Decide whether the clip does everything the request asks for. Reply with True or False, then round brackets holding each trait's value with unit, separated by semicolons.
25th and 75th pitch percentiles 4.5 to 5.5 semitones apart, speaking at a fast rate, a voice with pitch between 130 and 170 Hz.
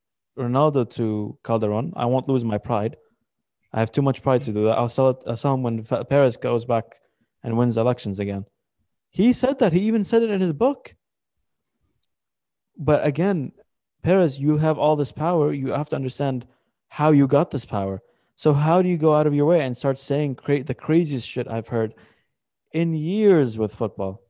True (5.1 semitones; 190 wpm; 135 Hz)